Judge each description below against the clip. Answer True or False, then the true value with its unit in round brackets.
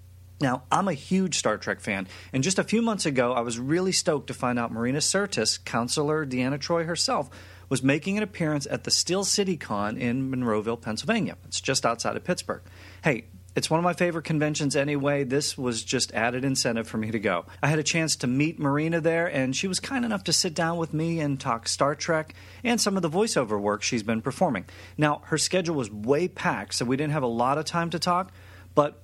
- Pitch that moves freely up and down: True (6.4 semitones)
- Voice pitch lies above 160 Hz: False (140 Hz)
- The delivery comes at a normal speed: False (225 wpm)